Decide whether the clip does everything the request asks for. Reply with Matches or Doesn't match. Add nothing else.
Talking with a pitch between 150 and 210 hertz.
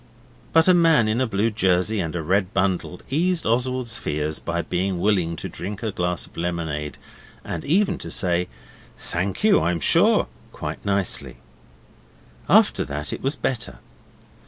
Doesn't match